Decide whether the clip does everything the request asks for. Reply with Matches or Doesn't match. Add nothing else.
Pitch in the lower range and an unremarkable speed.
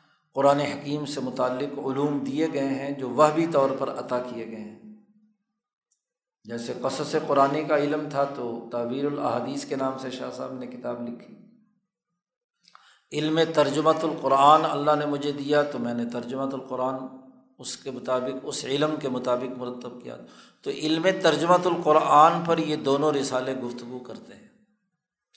Doesn't match